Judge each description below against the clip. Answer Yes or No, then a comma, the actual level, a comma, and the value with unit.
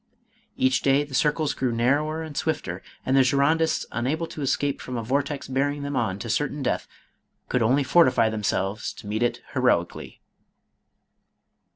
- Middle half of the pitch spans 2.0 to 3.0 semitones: No, average, 3.7 semitones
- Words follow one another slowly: No, average, 170 wpm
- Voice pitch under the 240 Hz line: Yes, low, 135 Hz